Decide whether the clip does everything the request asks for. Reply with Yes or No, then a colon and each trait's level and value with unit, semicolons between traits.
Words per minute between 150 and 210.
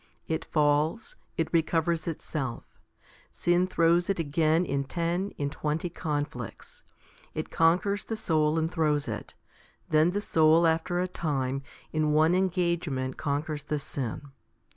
No: slow, 135 wpm